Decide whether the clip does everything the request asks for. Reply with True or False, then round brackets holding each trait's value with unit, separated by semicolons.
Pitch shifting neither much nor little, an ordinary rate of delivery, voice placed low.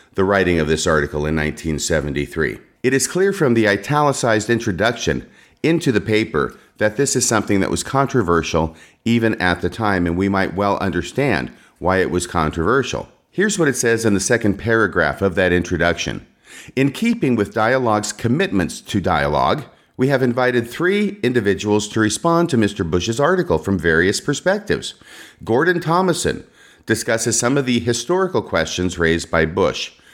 False (6.7 semitones; 160 wpm; 110 Hz)